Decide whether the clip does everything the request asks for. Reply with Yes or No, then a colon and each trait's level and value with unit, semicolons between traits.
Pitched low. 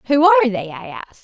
No: high, 210 Hz